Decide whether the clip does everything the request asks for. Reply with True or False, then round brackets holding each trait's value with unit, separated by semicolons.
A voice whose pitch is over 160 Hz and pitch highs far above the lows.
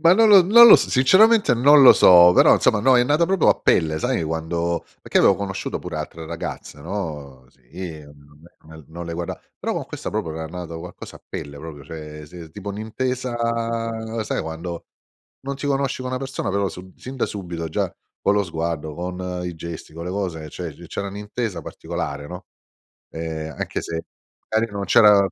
False (90 Hz; 6.2 semitones)